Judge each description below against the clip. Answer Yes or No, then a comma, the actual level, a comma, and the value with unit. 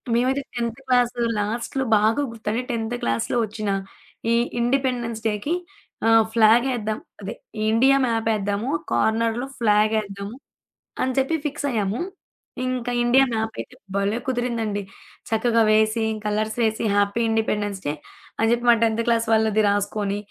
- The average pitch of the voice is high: Yes, high, 225 Hz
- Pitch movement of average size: No, narrow, 2.2 semitones